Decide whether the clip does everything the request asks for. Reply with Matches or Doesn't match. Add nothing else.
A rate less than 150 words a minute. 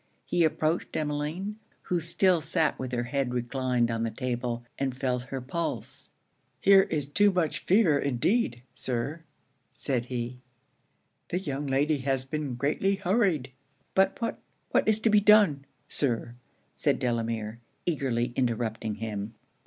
Matches